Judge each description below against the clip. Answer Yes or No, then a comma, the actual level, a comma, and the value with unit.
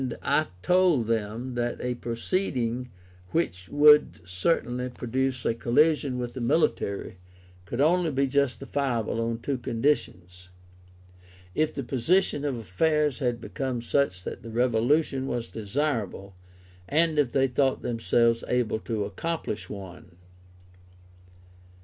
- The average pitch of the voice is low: Yes, low, 125 Hz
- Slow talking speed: Yes, slow, 120 wpm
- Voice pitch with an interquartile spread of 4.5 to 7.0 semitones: No, average, 4.1 semitones